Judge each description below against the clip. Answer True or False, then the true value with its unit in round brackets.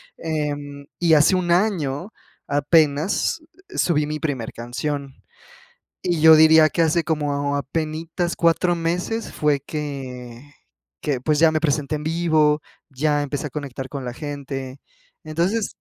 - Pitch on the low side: False (150 Hz)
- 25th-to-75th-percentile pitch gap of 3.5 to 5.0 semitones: False (2.5 semitones)